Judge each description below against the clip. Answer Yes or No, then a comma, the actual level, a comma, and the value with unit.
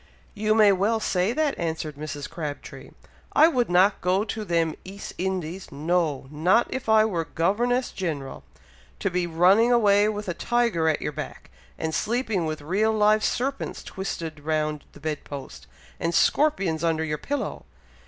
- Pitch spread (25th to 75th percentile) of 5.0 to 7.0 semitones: Yes, average, 5.3 semitones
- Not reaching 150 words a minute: No, average, 165 wpm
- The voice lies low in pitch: No, medium, 180 Hz